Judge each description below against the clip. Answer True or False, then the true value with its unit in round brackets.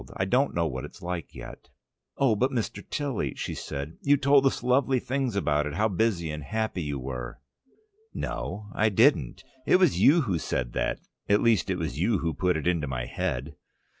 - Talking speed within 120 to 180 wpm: False (195 wpm)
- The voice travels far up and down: True (8.5 semitones)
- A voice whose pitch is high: False (95 Hz)